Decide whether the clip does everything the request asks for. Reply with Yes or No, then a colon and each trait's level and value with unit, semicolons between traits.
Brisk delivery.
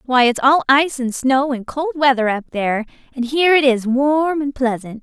Yes: fast, 225 wpm